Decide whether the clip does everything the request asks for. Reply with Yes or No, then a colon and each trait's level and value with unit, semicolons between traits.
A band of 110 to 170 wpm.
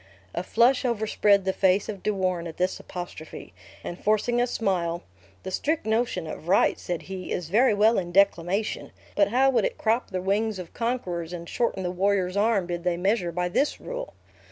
No: average, 195 wpm